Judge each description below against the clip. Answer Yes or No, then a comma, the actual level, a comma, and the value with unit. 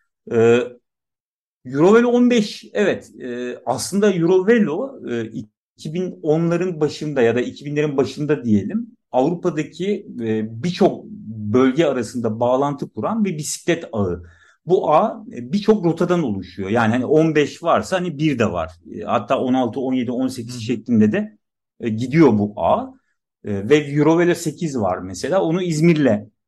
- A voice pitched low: No, medium, 150 Hz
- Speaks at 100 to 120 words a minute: Yes, average, 115 wpm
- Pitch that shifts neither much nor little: No, wide, 7.1 semitones